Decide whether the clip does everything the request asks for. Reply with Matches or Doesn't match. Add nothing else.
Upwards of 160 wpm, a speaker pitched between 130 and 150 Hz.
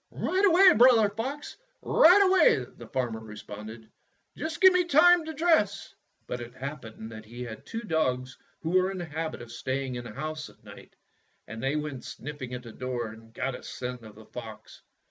Matches